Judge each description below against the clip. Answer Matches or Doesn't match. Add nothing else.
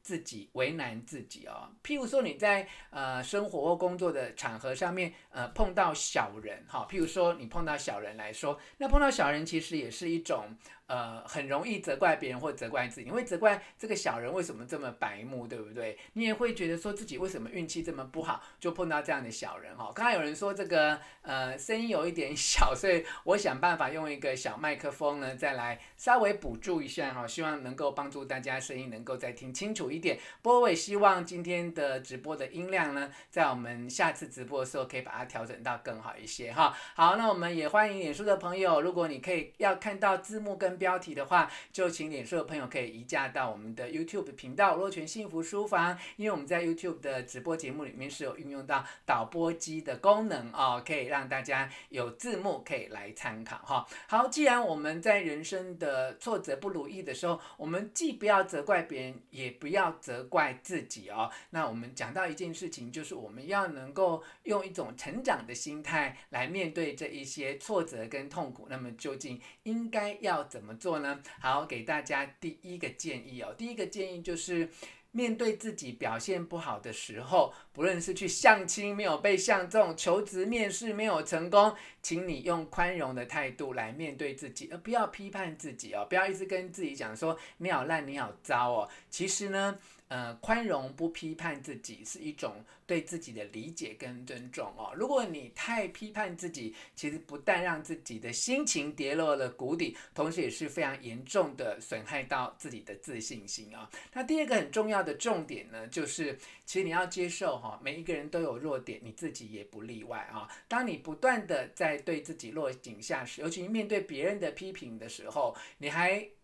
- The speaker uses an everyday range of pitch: Doesn't match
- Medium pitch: Matches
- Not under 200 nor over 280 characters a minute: Doesn't match